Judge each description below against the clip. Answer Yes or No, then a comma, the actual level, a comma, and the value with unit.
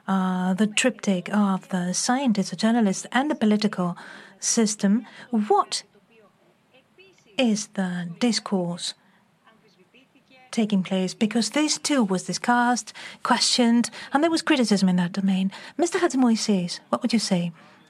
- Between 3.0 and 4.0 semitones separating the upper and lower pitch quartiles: No, average, 4.4 semitones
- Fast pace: No, average, 125 wpm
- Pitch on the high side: Yes, high, 215 Hz